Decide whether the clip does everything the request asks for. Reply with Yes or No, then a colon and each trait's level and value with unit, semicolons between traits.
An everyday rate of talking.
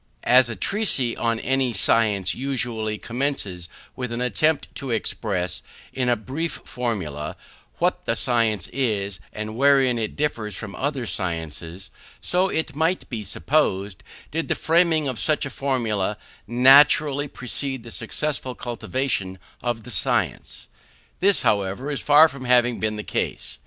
Yes: average, 145 wpm